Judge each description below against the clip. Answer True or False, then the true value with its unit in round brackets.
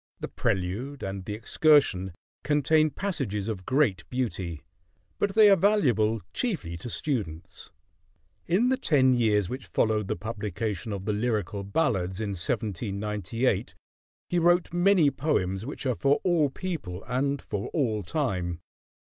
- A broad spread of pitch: True (7.1 semitones)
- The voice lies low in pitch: True (115 Hz)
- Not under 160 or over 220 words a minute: False (140 wpm)